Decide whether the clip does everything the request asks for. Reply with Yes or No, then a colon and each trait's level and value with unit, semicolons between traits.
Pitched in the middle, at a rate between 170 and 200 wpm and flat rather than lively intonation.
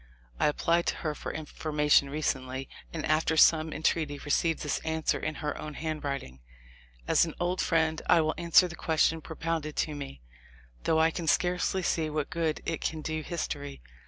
Yes: medium, 155 Hz; average, 180 wpm; narrow, 1.7 semitones